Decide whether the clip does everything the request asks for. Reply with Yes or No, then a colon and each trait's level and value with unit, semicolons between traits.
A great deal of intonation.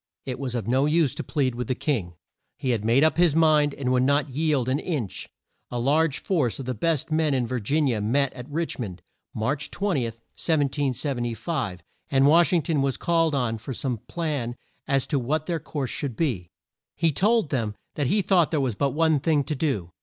No: average, 4.2 semitones